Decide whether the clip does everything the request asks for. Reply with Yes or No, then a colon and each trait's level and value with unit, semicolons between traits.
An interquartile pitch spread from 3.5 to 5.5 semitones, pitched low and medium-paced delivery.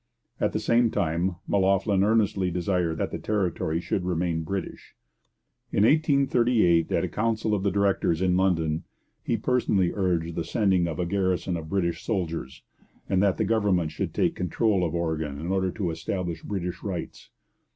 No: average, 3.1 semitones; very low, 95 Hz; average, 165 wpm